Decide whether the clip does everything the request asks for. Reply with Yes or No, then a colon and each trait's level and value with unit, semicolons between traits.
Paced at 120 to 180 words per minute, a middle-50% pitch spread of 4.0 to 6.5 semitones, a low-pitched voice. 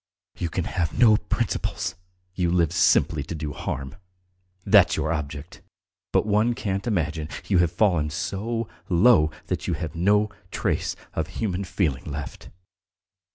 Yes: average, 145 wpm; average, 4.9 semitones; very low, 85 Hz